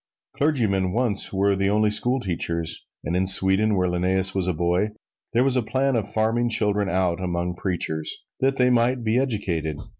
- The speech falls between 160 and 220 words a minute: Yes, average, 175 wpm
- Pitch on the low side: Yes, low, 100 Hz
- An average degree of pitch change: Yes, average, 4.5 semitones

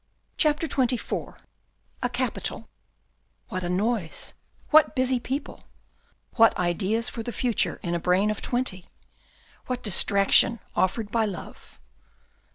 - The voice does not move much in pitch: No, average, 5.0 semitones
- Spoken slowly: Yes, slow, 125 wpm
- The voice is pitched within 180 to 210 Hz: No, high, 225 Hz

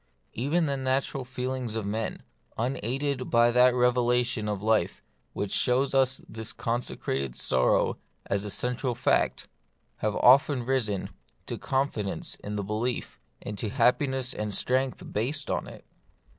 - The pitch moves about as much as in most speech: Yes, average, 3.6 semitones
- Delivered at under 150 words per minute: Yes, average, 140 wpm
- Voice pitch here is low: Yes, low, 125 Hz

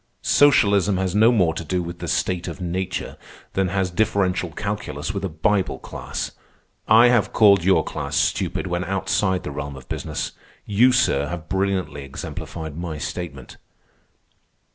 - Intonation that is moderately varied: Yes, average, 3.4 semitones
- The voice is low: Yes, very low, 90 Hz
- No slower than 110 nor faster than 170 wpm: Yes, average, 155 wpm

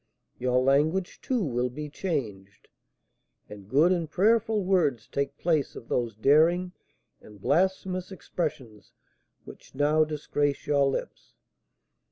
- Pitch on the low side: No, medium, 150 Hz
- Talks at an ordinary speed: No, slow, 120 wpm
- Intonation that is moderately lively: No, wide, 5.8 semitones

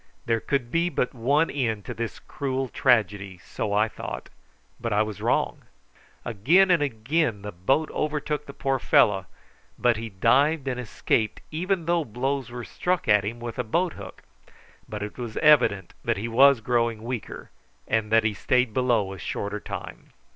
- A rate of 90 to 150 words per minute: No, average, 175 wpm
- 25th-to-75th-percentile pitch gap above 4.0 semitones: Yes, average, 4.7 semitones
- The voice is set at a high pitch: No, low, 120 Hz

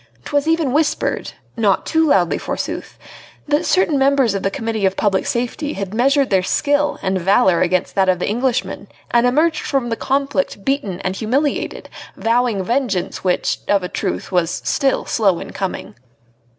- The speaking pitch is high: Yes, high, 235 Hz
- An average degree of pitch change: No, wide, 6.5 semitones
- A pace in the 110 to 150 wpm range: No, average, 165 wpm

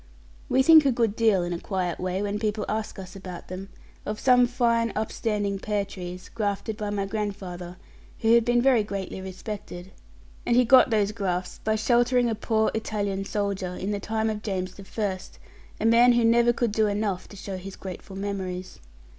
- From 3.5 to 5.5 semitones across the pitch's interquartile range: No, average, 3.0 semitones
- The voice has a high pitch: Yes, high, 205 Hz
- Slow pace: No, average, 190 wpm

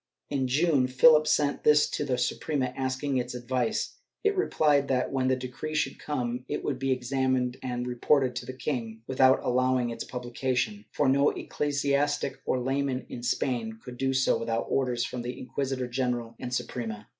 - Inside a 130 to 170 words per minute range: No, average, 180 wpm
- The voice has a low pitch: Yes, low, 130 Hz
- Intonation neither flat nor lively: No, narrow, 2.2 semitones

